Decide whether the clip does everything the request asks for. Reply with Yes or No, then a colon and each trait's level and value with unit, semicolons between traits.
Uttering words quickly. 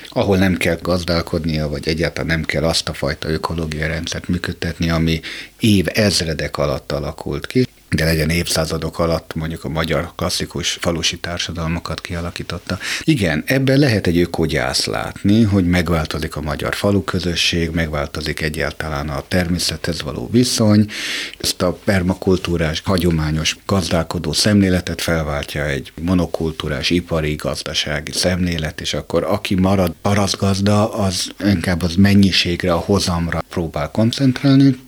No: average, 125 wpm